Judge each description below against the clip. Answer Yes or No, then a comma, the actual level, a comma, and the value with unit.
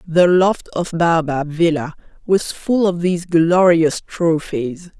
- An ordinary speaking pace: No, slow, 130 wpm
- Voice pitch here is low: No, medium, 170 Hz